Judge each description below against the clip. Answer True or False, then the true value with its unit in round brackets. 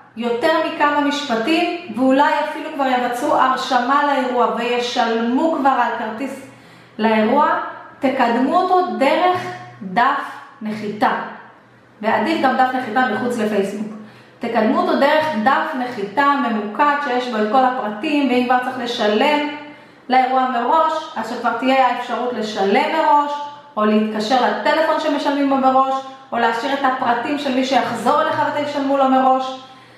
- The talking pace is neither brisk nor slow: True (130 wpm)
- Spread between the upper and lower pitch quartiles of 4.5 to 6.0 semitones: False (3.8 semitones)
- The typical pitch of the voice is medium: False (260 Hz)